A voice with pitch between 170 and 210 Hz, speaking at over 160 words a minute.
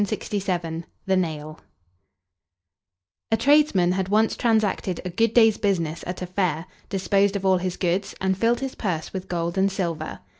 No: high, 190 Hz; average, 155 wpm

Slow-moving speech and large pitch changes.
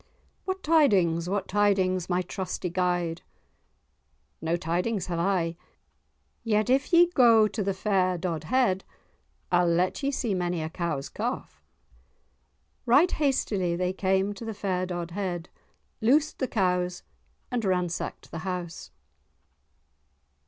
No: slow, 120 wpm; average, 3.7 semitones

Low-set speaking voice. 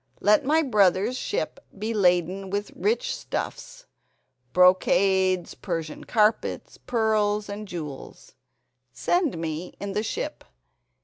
No: high, 205 Hz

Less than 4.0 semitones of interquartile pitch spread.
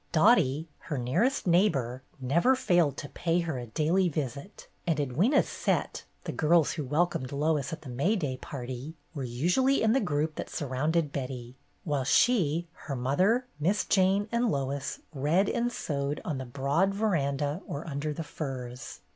No: average, 4.8 semitones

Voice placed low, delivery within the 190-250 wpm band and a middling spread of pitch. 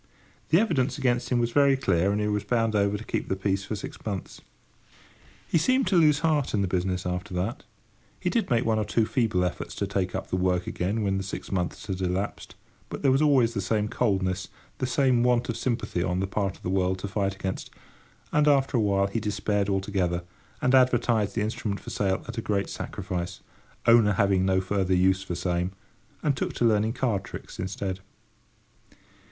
Yes: low, 100 Hz; average, 200 wpm; average, 4.1 semitones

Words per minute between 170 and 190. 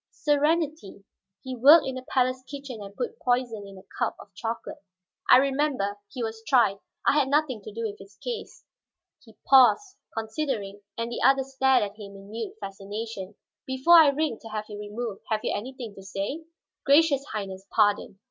Yes: average, 180 wpm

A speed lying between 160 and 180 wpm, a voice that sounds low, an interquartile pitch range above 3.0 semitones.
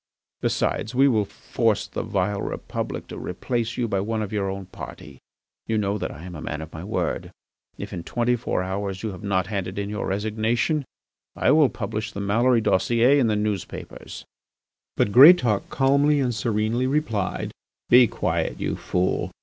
Yes: average, 175 wpm; low, 110 Hz; average, 3.6 semitones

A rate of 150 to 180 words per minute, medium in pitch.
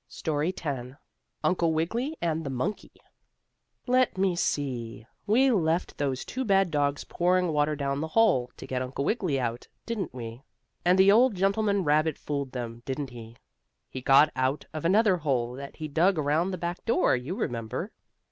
Yes: average, 175 wpm; medium, 155 Hz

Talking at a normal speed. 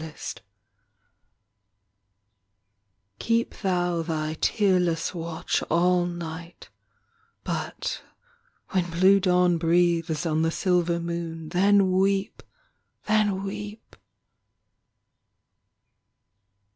No: slow, 80 wpm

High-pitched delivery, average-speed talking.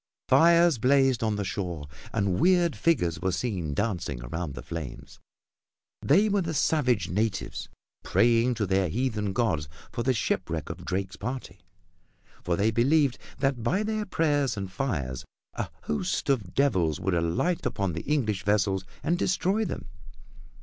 No: low, 110 Hz; average, 150 wpm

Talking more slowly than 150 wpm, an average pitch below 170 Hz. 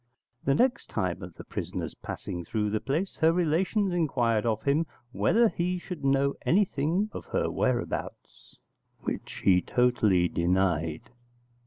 Yes: average, 140 wpm; low, 135 Hz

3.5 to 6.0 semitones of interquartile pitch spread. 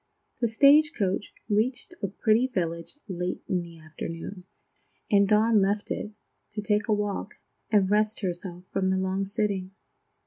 No: narrow, 2.6 semitones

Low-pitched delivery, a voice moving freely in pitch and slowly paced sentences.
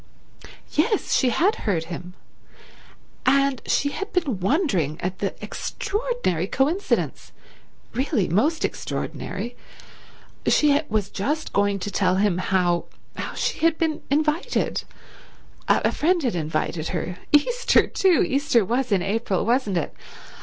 No: high, 240 Hz; wide, 8.6 semitones; slow, 110 wpm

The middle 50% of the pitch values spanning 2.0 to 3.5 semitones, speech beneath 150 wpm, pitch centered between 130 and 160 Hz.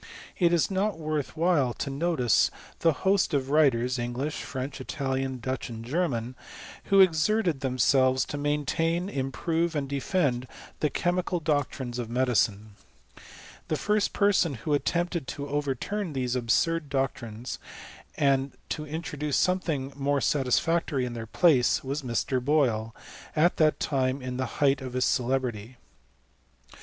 No: average, 4.2 semitones; average, 140 wpm; medium, 140 Hz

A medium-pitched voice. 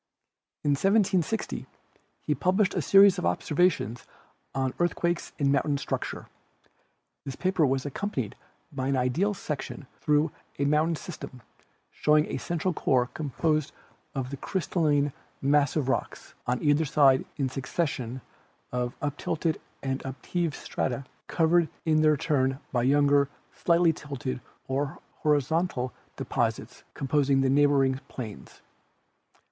Yes: medium, 145 Hz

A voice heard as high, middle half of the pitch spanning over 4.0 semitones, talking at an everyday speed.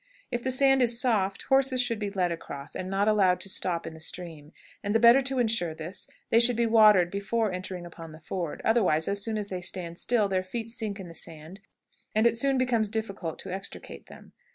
No: high, 200 Hz; average, 4.6 semitones; fast, 225 wpm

